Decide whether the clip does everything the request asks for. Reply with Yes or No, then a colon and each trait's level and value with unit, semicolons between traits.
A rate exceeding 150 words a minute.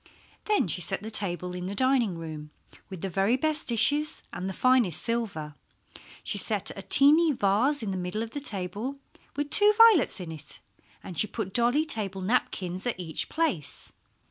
Yes: average, 180 wpm